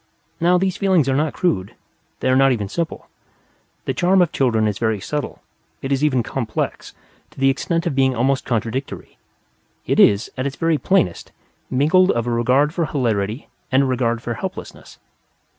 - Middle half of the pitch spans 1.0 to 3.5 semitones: No, average, 4.6 semitones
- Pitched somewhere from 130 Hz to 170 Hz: Yes, low, 135 Hz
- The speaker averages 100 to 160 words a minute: No, average, 175 wpm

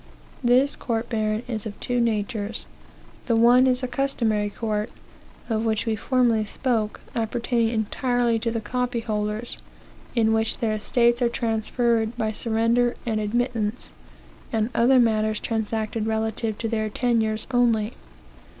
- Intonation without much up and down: Yes, narrow, 1.9 semitones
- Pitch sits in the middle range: No, high, 225 Hz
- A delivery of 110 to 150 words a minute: Yes, average, 140 wpm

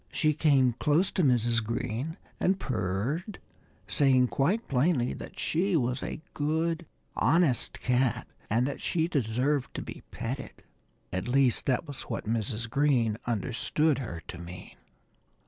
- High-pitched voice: No, low, 130 Hz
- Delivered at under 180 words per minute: Yes, average, 140 wpm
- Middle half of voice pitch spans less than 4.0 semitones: No, average, 4.8 semitones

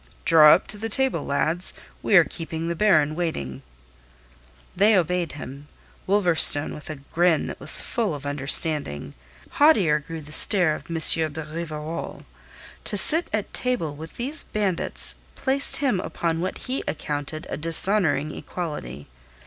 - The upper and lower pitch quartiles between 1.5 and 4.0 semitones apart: No, average, 4.6 semitones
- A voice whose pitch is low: No, medium, 165 Hz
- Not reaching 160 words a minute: Yes, average, 150 wpm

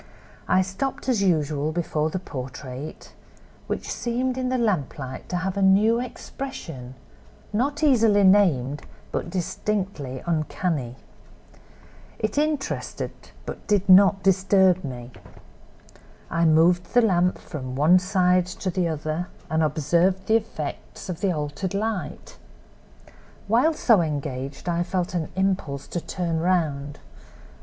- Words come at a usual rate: No, slow, 125 wpm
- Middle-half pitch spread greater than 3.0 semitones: Yes, average, 4.6 semitones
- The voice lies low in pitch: No, medium, 180 Hz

